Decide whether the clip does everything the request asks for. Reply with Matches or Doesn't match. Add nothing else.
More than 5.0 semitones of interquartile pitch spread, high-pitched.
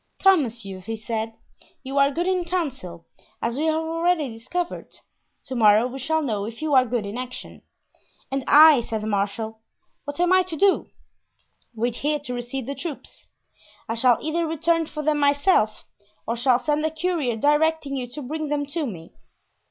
Matches